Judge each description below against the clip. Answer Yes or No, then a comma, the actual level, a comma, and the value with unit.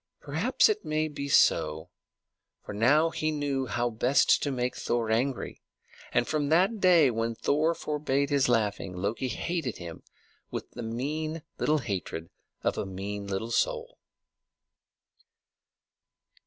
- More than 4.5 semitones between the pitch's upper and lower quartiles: Yes, wide, 5.4 semitones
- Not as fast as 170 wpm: Yes, slow, 135 wpm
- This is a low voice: Yes, low, 130 Hz